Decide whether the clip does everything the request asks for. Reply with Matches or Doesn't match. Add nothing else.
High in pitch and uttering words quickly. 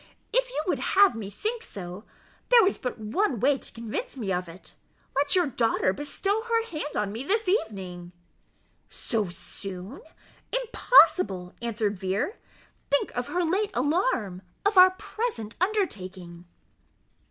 Doesn't match